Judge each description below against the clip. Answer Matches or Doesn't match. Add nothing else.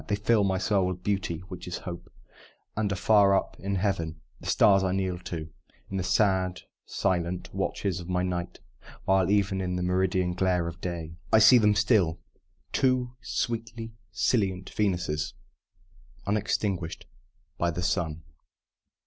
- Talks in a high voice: Doesn't match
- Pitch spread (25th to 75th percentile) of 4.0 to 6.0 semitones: Doesn't match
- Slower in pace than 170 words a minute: Matches